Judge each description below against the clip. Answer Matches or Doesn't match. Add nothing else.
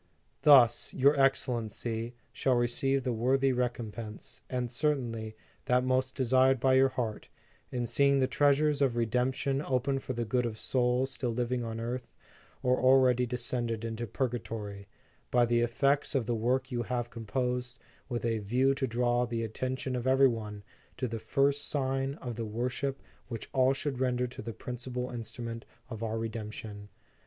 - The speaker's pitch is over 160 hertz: Doesn't match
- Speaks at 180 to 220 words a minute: Doesn't match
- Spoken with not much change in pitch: Matches